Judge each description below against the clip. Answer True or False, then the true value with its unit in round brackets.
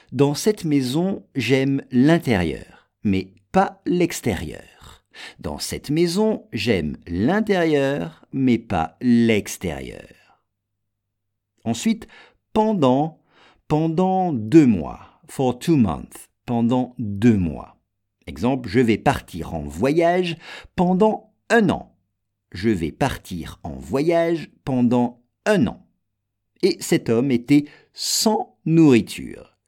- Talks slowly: True (100 wpm)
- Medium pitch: False (125 Hz)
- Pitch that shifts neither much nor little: False (8.3 semitones)